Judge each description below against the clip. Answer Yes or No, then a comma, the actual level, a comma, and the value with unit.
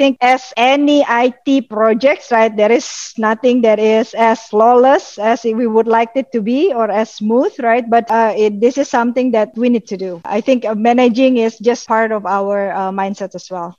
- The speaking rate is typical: No, fast, 215 wpm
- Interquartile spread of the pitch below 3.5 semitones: Yes, narrow, 2.4 semitones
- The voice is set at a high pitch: Yes, high, 230 Hz